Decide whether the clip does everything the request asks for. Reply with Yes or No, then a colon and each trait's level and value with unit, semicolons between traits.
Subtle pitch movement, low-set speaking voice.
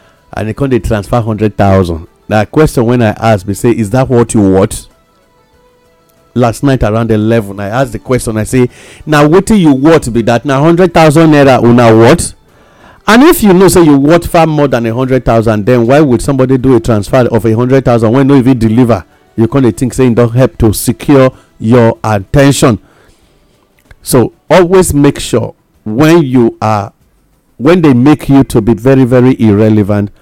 No: average, 3.8 semitones; low, 125 Hz